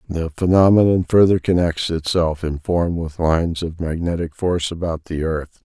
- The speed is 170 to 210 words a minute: No, average, 160 wpm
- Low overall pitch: Yes, very low, 85 Hz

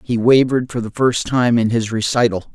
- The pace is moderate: No, fast, 210 wpm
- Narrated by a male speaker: Yes, male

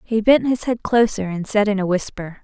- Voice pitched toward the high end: Yes, high, 210 Hz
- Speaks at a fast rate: Yes, fast, 245 wpm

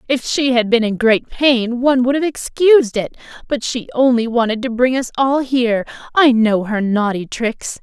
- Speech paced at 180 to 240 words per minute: Yes, average, 200 wpm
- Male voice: No, female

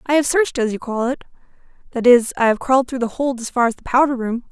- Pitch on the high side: Yes, very high, 250 Hz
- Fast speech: Yes, fast, 265 wpm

